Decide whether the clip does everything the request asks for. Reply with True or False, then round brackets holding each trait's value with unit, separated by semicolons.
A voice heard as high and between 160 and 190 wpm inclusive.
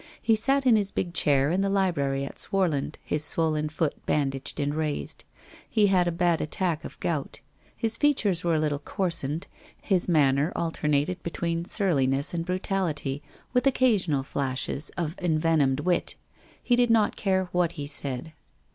False (165 Hz; 165 wpm)